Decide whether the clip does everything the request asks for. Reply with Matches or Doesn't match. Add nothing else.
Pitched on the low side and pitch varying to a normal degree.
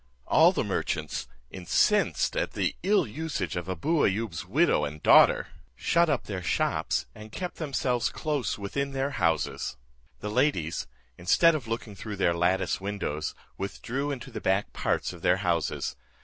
Doesn't match